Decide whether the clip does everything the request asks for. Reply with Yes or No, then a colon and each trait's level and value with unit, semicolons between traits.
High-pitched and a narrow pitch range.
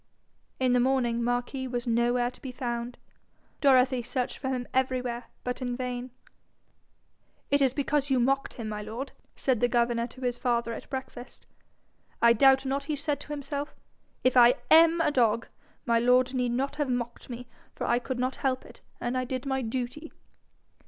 Yes: very high, 250 Hz; narrow, 1.7 semitones